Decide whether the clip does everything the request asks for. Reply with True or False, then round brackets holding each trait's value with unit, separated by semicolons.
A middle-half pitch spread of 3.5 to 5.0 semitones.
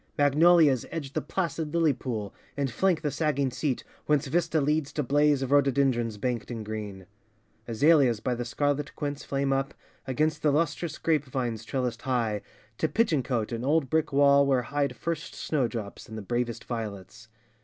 True (4.0 semitones)